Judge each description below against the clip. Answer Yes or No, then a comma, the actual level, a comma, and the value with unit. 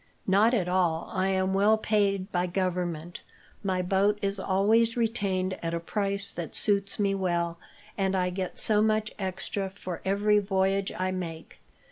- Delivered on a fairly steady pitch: Yes, narrow, 1.9 semitones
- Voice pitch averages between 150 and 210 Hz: Yes, high, 190 Hz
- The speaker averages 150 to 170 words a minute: Yes, average, 160 wpm